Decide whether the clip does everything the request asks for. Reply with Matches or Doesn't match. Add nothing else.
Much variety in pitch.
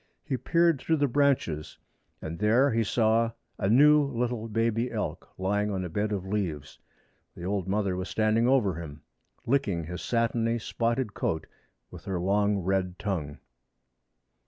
Doesn't match